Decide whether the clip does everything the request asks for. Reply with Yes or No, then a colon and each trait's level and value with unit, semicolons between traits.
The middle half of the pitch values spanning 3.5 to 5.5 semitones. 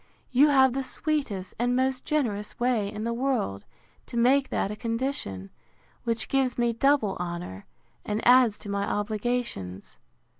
Yes: average, 4.4 semitones